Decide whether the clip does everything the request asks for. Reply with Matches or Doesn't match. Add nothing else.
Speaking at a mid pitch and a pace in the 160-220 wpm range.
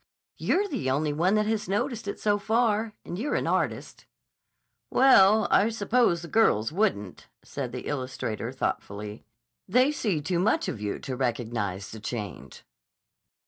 Doesn't match